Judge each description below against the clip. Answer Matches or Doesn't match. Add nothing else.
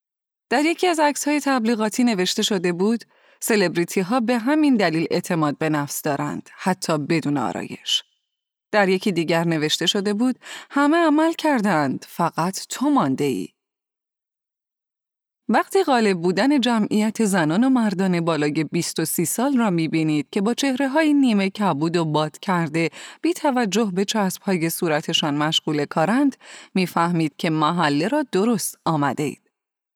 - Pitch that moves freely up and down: Matches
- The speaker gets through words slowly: Doesn't match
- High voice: Matches